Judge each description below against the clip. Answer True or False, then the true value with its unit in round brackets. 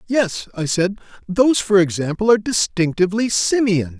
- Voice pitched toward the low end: False (195 Hz)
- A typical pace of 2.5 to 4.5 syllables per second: False (5.2 syllables/s)